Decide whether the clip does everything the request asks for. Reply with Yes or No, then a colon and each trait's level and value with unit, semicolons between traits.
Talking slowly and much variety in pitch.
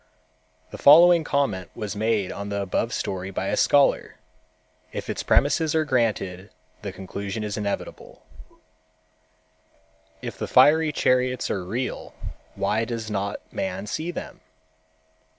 Yes: slow, 130 wpm; wide, 6.0 semitones